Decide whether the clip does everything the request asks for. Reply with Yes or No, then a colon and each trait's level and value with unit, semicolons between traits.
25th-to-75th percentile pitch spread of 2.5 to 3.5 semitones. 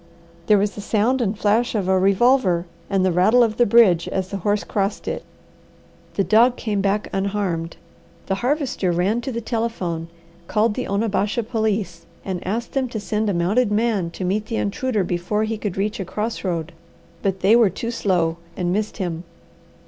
Yes: average, 3.2 semitones